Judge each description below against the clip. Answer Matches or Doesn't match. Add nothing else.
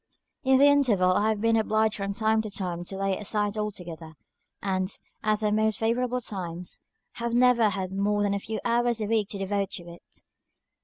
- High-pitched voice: Matches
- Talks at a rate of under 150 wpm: Doesn't match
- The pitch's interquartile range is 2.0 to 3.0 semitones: Matches